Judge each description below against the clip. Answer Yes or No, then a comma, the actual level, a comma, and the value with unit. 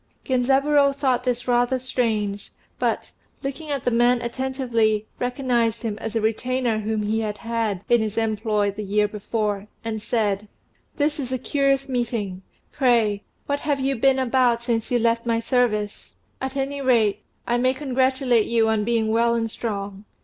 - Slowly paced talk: No, average, 165 wpm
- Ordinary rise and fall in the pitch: Yes, average, 3.2 semitones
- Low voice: No, high, 235 Hz